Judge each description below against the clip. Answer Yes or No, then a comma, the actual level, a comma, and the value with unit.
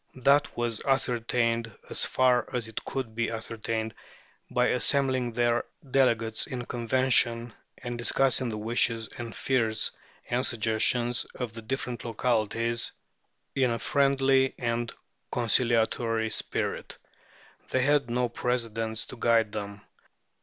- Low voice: Yes, low, 120 Hz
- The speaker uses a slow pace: Yes, slow, 120 wpm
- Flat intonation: Yes, narrow, 1.8 semitones